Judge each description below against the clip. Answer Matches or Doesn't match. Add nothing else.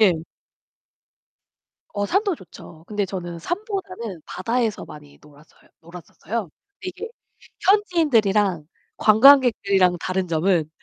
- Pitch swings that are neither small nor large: Doesn't match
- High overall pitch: Matches